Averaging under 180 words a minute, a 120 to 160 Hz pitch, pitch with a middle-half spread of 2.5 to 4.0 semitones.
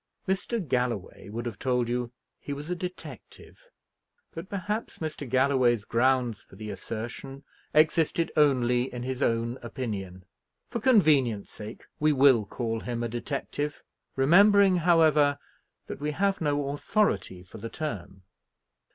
No: slow, 135 wpm; low, 135 Hz; average, 5.1 semitones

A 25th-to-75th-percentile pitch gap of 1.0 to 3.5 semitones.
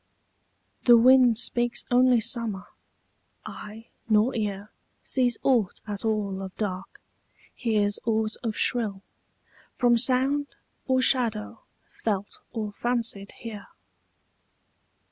Yes: average, 2.8 semitones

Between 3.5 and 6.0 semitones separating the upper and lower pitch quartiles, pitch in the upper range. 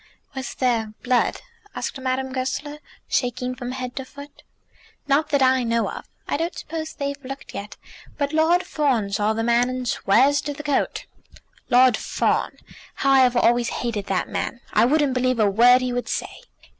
No: average, 2.7 semitones; very high, 255 Hz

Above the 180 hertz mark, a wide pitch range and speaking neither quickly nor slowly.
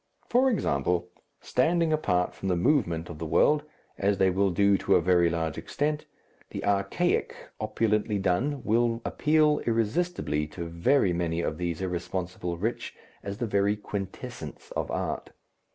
No: low, 100 Hz; wide, 5.7 semitones; average, 150 wpm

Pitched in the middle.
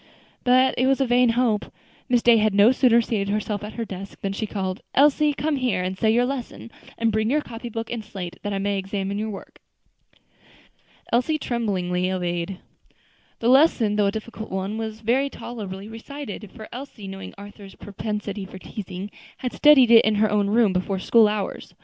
No: high, 215 Hz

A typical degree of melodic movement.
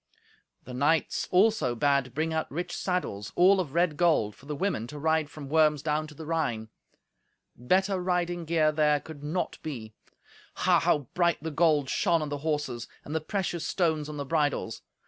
Yes: average, 3.2 semitones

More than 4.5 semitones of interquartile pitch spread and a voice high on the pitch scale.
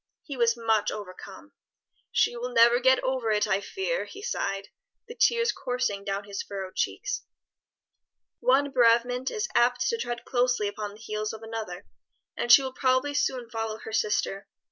No: average, 3.5 semitones; high, 235 Hz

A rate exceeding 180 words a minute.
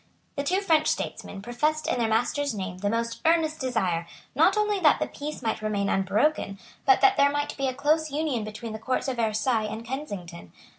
Yes: average, 200 wpm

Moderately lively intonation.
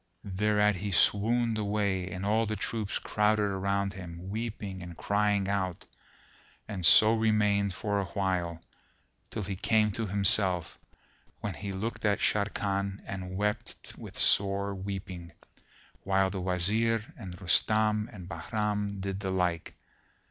No: narrow, 2.0 semitones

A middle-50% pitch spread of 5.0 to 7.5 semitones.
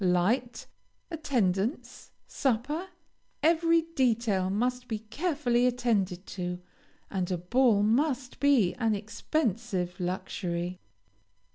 Yes: wide, 5.6 semitones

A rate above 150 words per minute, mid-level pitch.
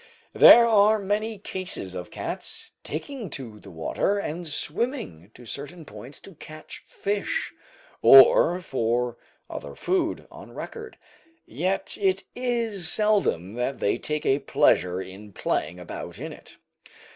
No: slow, 135 wpm; medium, 160 Hz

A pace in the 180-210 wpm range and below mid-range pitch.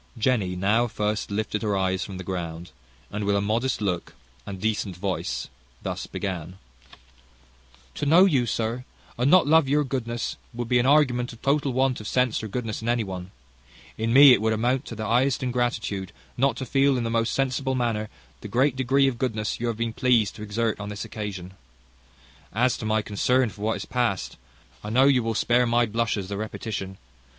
Yes: average, 195 wpm; low, 115 Hz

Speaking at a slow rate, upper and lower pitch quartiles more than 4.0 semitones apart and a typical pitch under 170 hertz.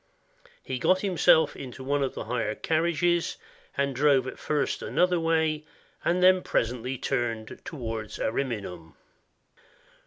Yes: slow, 120 wpm; wide, 5.4 semitones; medium, 140 Hz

